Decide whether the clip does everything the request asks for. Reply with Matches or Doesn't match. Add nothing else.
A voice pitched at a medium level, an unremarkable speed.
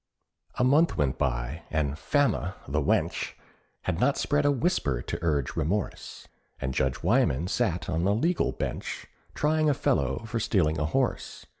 Doesn't match